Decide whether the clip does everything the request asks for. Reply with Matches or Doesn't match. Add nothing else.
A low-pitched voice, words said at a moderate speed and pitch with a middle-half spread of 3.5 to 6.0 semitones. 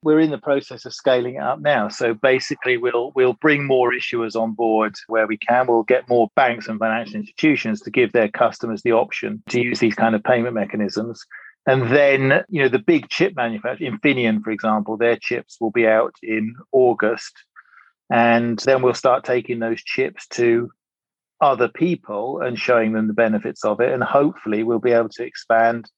Doesn't match